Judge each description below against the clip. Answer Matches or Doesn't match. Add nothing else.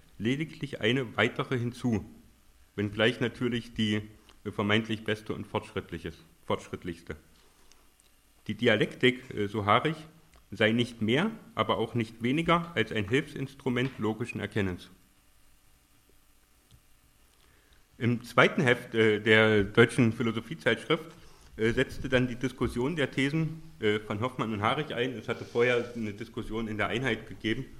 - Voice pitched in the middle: Doesn't match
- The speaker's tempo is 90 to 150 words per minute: Matches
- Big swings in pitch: Doesn't match